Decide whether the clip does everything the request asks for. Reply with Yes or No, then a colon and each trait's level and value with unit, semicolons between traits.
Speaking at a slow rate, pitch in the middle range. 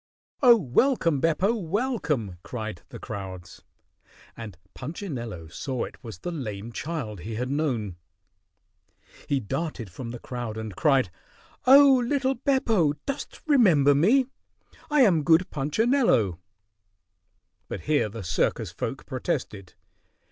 Yes: slow, 120 wpm; medium, 145 Hz